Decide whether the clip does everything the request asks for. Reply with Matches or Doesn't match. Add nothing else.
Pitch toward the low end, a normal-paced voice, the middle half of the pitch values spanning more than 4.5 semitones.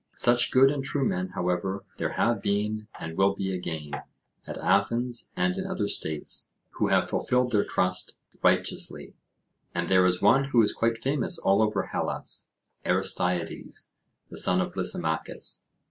Matches